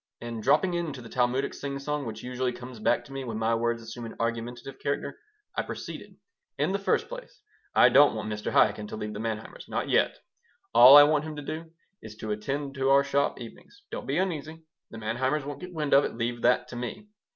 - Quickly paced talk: Yes, fast, 220 wpm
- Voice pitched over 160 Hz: No, low, 130 Hz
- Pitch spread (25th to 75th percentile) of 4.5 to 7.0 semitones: No, average, 4.1 semitones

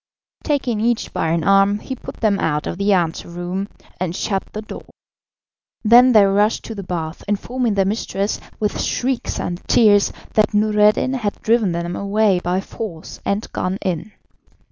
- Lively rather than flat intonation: No, average, 3.0 semitones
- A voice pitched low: No, high, 200 Hz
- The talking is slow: No, average, 165 wpm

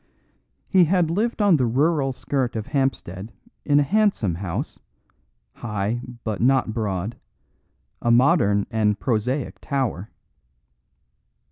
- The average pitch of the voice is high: No, low, 125 Hz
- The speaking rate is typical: No, slow, 115 wpm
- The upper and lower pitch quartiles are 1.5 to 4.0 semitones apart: No, wide, 5.5 semitones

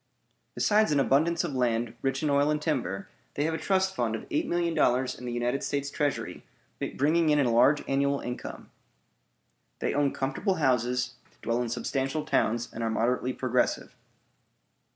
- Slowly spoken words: No, average, 170 wpm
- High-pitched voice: No, low, 135 Hz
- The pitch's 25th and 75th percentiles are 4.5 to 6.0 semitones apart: No, average, 3.6 semitones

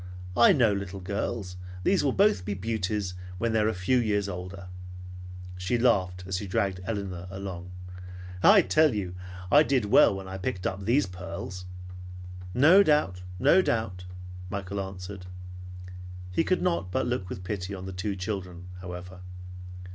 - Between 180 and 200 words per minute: No, average, 160 wpm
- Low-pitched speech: Yes, low, 100 Hz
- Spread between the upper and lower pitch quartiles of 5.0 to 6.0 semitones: No, average, 3.8 semitones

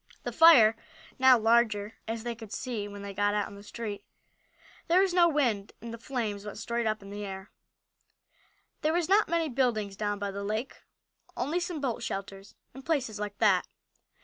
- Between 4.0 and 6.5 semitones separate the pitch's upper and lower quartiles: Yes, average, 4.4 semitones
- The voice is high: Yes, high, 225 Hz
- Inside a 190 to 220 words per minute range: Yes, average, 195 wpm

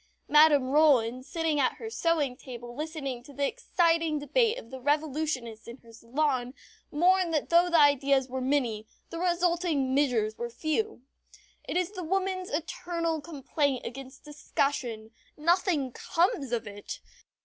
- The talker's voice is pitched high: Yes, very high, 290 Hz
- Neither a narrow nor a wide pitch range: Yes, average, 4.7 semitones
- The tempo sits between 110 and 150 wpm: Yes, average, 145 wpm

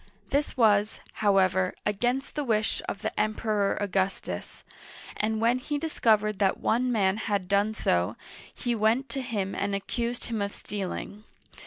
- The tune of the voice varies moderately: Yes, average, 3.0 semitones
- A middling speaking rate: Yes, average, 150 wpm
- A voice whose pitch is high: Yes, high, 215 Hz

